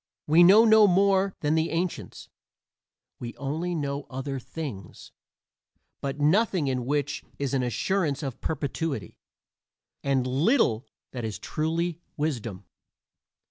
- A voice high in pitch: No, medium, 145 Hz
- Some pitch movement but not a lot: Yes, average, 4.6 semitones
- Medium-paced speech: No, slow, 120 wpm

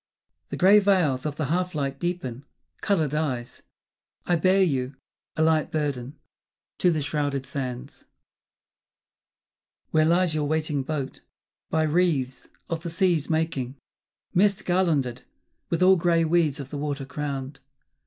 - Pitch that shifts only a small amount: No, average, 3.9 semitones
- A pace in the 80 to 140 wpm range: Yes, slow, 135 wpm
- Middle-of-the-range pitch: Yes, medium, 155 Hz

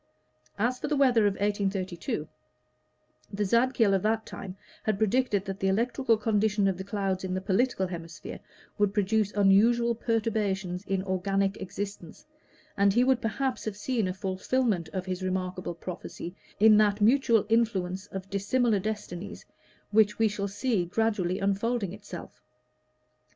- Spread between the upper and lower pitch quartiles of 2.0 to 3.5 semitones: Yes, average, 2.8 semitones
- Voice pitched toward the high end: Yes, high, 205 Hz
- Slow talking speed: No, average, 145 wpm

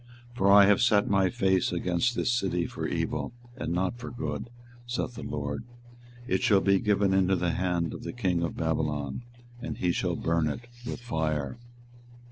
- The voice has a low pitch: Yes, very low, 95 Hz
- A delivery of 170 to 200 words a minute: Yes, average, 185 wpm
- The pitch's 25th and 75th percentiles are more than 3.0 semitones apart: Yes, average, 4.0 semitones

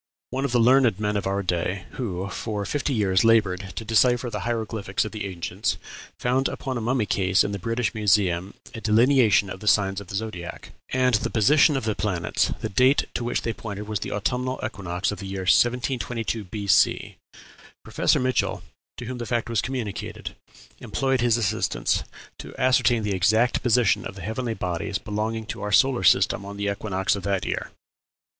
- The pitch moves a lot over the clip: No, average, 3.7 semitones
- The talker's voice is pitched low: Yes, low, 110 Hz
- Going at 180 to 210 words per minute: Yes, average, 190 wpm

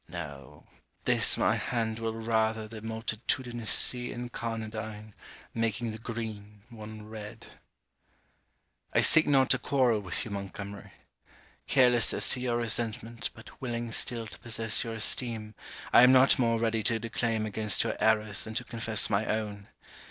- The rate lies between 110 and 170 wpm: Yes, average, 150 wpm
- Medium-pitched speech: No, low, 110 Hz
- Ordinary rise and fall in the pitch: No, narrow, 1.6 semitones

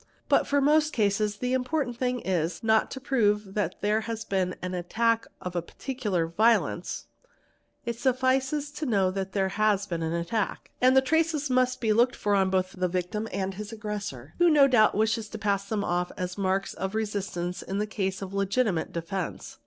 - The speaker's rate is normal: Yes, average, 195 wpm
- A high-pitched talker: Yes, high, 210 Hz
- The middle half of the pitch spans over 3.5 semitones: Yes, average, 4.8 semitones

